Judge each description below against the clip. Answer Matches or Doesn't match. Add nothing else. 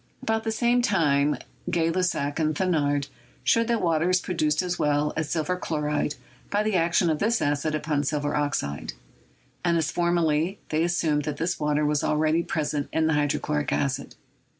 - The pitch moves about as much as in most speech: Matches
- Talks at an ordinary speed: Matches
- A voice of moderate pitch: Matches